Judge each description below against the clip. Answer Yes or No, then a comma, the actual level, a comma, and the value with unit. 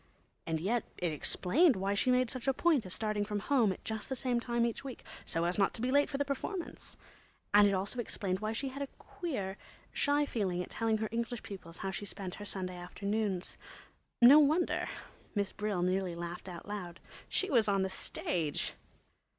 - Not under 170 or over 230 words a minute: Yes, average, 200 wpm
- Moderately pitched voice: No, high, 210 Hz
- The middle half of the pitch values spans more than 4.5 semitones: Yes, average, 5.1 semitones